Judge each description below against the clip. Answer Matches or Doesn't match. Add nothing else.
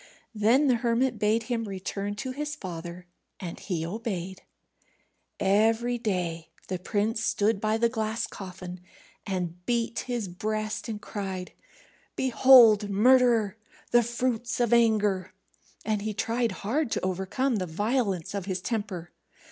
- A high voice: Matches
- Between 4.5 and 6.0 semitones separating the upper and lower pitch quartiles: Doesn't match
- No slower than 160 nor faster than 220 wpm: Doesn't match